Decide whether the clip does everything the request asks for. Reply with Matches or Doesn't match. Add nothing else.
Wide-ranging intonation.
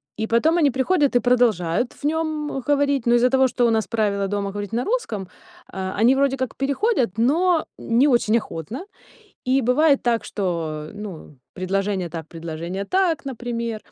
Matches